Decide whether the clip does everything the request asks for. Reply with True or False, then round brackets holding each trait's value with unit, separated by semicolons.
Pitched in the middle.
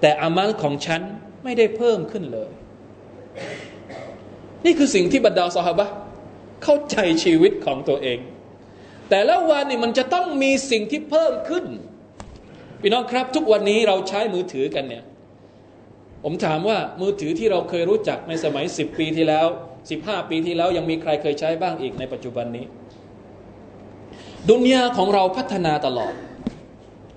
True (180 Hz)